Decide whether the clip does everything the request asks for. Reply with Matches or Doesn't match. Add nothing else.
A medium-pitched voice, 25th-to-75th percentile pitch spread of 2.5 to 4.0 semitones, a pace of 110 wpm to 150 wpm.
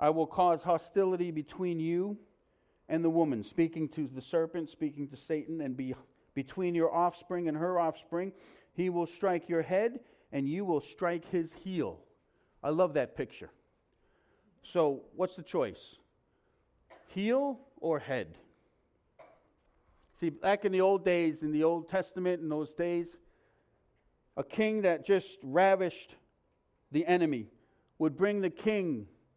Matches